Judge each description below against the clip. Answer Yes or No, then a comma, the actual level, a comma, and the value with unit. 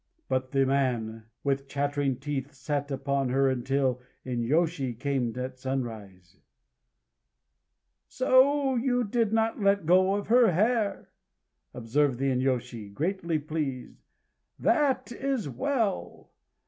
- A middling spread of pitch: No, wide, 7.6 semitones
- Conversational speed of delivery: No, slow, 115 wpm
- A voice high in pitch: No, medium, 140 Hz